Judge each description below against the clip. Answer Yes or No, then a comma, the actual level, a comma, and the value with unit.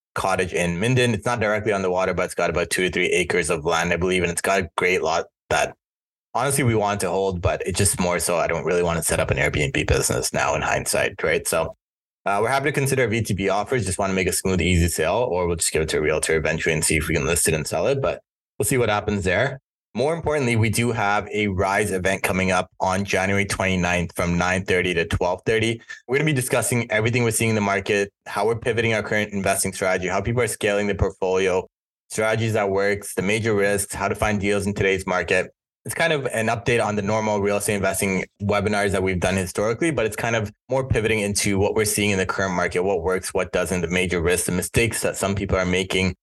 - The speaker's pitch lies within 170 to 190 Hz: No, low, 100 Hz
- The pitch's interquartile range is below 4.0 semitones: Yes, average, 2.8 semitones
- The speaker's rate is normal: No, fast, 250 wpm